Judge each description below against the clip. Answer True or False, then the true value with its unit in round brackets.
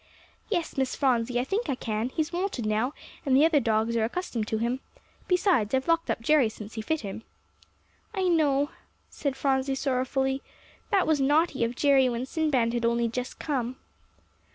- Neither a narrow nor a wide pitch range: True (4.6 semitones)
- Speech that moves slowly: False (175 wpm)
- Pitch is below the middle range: False (265 Hz)